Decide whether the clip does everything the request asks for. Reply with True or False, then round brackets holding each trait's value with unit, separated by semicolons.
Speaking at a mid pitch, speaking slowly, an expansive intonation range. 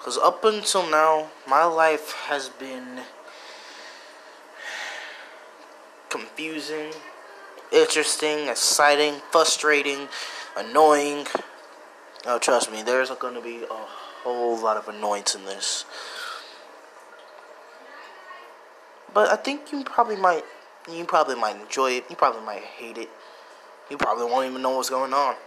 True (150 Hz; 120 wpm; 6.1 semitones)